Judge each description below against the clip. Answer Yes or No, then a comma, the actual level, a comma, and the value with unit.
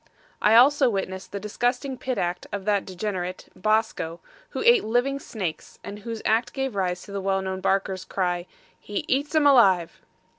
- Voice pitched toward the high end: Yes, high, 205 Hz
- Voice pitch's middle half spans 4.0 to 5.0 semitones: Yes, average, 4.6 semitones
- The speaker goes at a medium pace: Yes, average, 175 wpm